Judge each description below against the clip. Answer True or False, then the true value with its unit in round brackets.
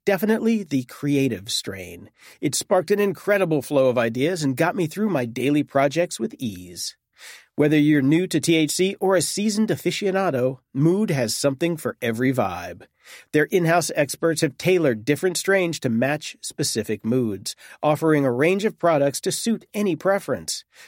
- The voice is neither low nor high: True (155 Hz)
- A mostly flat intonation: False (5.6 semitones)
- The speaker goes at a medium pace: True (160 wpm)